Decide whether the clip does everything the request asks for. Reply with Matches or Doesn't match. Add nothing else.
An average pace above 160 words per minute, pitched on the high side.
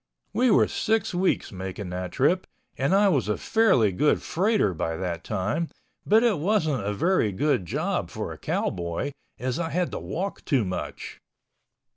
Doesn't match